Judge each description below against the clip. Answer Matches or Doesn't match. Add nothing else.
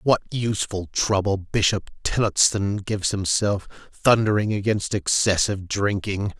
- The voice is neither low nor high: Doesn't match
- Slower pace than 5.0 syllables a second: Matches